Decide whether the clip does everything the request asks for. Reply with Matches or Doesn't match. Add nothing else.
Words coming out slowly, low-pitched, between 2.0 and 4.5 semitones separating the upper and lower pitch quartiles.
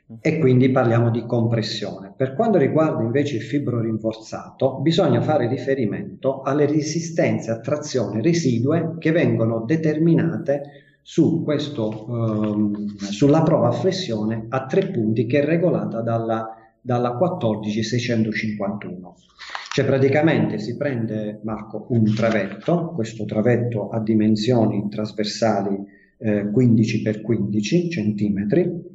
Doesn't match